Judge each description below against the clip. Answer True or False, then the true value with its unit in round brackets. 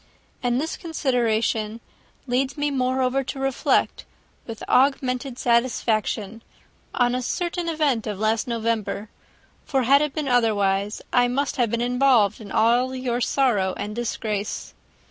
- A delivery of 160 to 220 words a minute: False (135 wpm)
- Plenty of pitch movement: False (3.3 semitones)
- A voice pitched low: False (245 Hz)